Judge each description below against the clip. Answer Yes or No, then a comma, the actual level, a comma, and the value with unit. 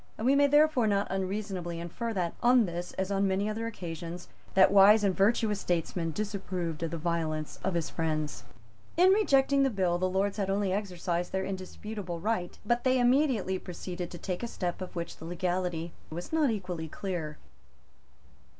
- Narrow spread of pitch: No, average, 3.8 semitones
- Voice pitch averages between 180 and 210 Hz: Yes, high, 190 Hz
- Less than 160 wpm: No, average, 175 wpm